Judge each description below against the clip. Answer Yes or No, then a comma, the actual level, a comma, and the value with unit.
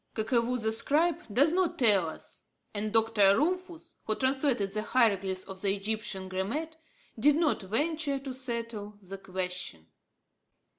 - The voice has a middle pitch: No, high, 225 Hz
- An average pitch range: No, wide, 6.2 semitones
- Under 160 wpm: Yes, average, 140 wpm